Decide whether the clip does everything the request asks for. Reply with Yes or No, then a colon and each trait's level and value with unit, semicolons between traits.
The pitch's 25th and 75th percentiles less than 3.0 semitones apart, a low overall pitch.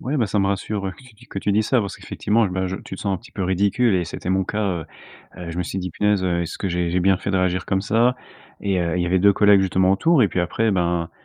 Yes: narrow, 2.4 semitones; very low, 95 Hz